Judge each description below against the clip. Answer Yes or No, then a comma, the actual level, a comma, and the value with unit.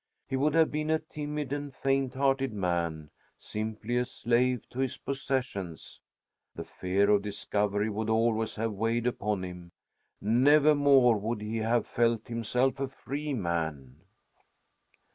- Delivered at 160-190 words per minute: No, average, 140 wpm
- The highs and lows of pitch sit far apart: No, average, 4.7 semitones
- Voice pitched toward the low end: Yes, low, 115 Hz